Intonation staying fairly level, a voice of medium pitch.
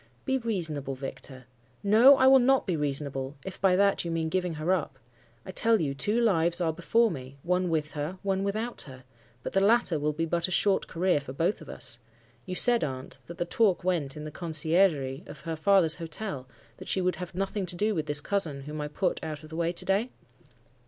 No: average, 4.6 semitones; medium, 170 Hz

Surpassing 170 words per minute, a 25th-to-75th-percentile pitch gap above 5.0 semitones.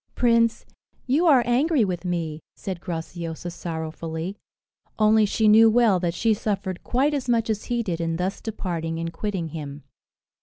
No: average, 160 wpm; wide, 5.6 semitones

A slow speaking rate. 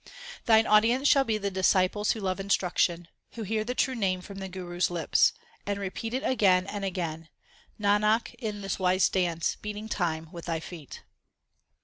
No: average, 175 wpm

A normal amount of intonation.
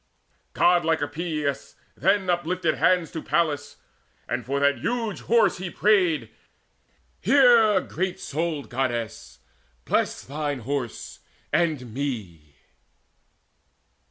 Yes: average, 4.6 semitones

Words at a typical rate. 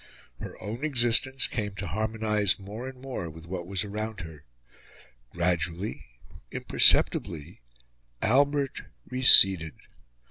No: slow, 105 wpm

